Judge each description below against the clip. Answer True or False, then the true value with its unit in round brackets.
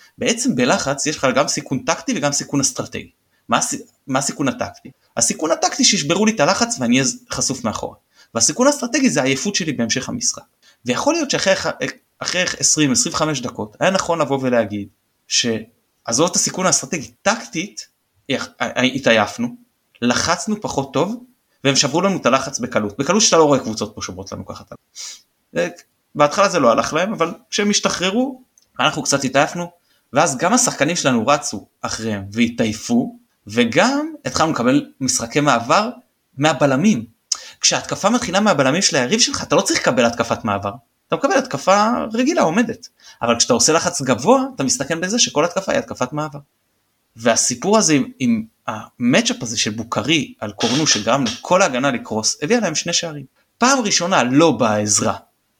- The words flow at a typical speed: False (155 wpm)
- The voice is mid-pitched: True (155 Hz)